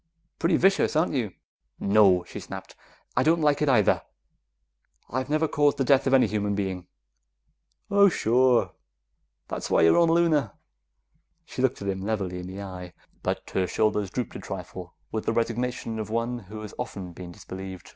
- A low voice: Yes, low, 110 Hz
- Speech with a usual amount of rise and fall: No, wide, 5.9 semitones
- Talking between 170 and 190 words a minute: Yes, average, 175 wpm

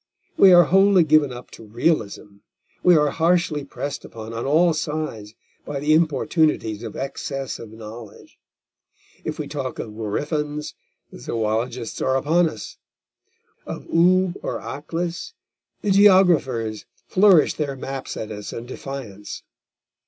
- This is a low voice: No, medium, 145 Hz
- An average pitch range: No, wide, 6.6 semitones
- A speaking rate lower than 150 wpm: Yes, slow, 135 wpm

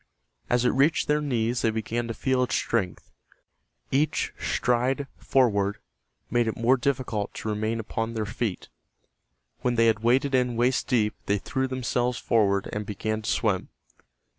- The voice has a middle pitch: No, low, 120 Hz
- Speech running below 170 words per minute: Yes, average, 160 wpm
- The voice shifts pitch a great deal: No, average, 2.8 semitones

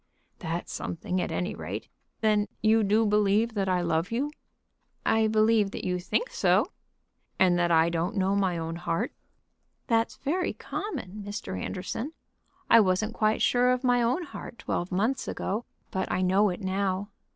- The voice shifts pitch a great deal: No, average, 3.8 semitones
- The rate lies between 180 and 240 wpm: No, average, 165 wpm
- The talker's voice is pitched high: Yes, high, 205 Hz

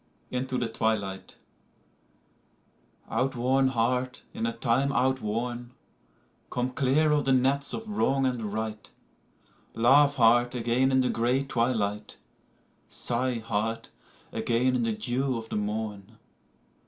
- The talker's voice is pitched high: No, low, 120 Hz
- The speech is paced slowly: Yes, slow, 130 wpm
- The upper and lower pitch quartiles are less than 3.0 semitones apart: Yes, narrow, 2.6 semitones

